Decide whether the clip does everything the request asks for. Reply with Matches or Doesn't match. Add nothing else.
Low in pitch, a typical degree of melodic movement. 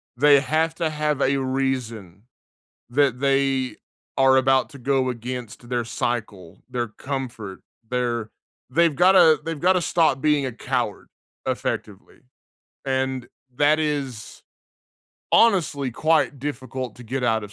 Matches